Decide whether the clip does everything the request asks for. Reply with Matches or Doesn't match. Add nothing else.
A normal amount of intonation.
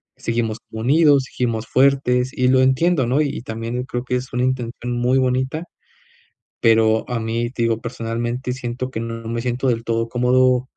Doesn't match